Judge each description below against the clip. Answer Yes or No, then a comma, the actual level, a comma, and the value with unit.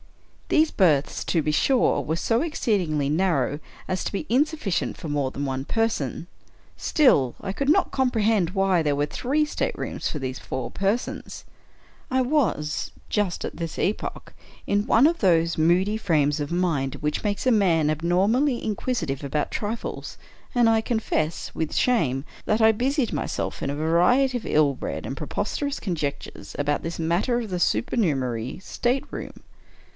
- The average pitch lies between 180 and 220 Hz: Yes, medium, 185 Hz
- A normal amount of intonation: No, wide, 7.6 semitones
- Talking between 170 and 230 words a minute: No, average, 160 wpm